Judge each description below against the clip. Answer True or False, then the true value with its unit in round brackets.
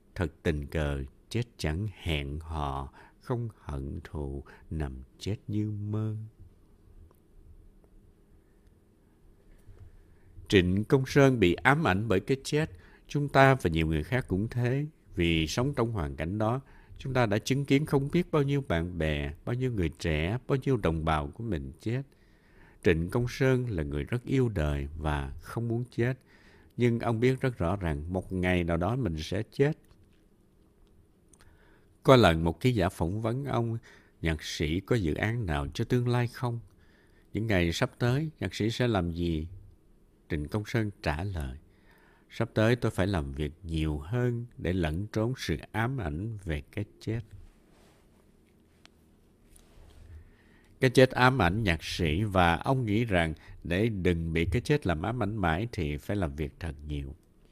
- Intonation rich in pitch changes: True (6.2 semitones)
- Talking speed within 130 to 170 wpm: True (165 wpm)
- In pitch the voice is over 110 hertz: False (95 Hz)